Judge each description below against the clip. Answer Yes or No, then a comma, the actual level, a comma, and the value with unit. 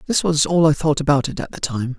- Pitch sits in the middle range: Yes, medium, 145 Hz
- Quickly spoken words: Yes, fast, 300 wpm